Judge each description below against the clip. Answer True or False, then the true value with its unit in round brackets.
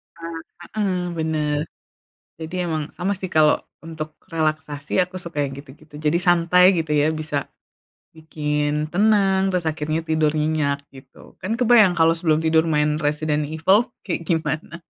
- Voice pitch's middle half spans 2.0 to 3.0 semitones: True (2.5 semitones)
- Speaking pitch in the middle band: True (160 Hz)